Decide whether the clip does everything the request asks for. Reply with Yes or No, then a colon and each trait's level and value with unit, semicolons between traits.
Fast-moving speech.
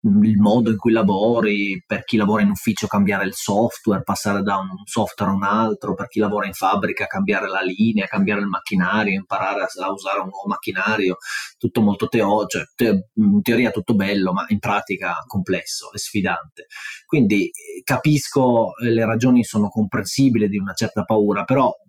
Yes: fast, 175 wpm